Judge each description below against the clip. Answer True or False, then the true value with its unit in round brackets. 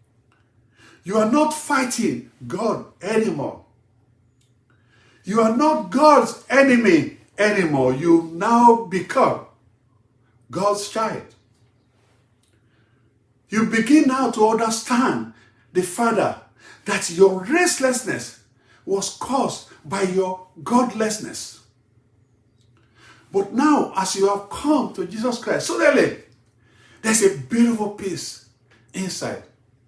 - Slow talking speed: True (95 wpm)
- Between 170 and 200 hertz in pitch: True (185 Hz)